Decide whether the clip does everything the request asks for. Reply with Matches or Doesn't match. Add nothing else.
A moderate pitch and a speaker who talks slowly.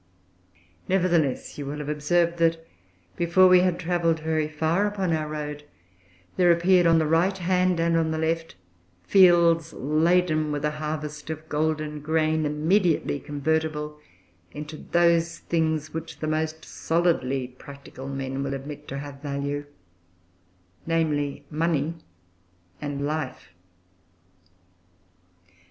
Matches